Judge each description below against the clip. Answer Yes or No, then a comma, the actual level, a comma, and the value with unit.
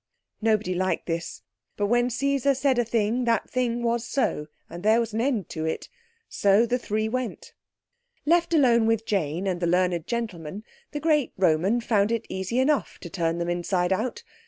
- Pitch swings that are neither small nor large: Yes, average, 4.9 semitones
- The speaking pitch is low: No, high, 220 Hz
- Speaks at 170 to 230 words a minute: Yes, average, 180 wpm